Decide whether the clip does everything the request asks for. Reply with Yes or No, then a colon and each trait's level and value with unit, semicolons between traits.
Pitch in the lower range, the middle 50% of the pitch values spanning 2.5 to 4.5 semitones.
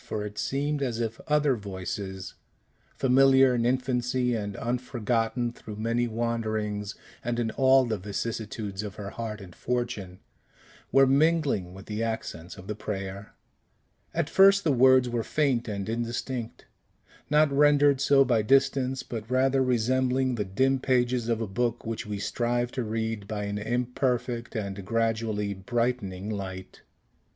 Yes: low, 115 Hz; average, 3.6 semitones